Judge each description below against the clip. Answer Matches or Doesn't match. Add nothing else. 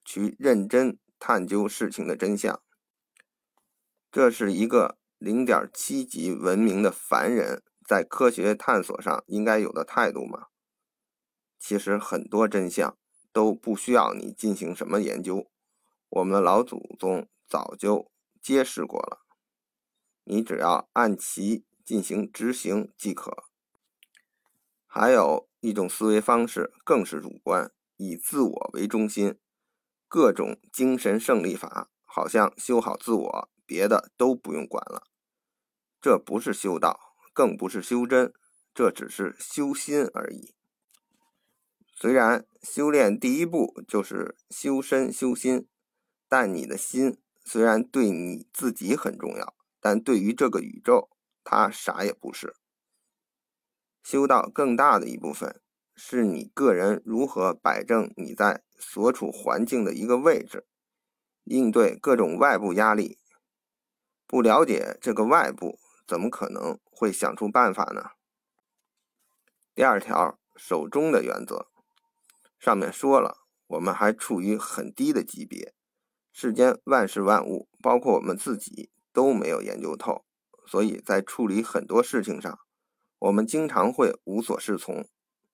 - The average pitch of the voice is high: Doesn't match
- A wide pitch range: Matches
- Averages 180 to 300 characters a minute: Matches